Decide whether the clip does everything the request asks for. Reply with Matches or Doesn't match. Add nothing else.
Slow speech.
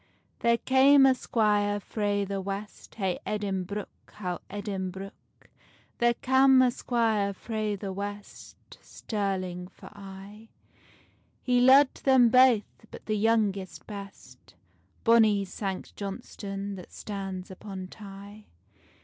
Matches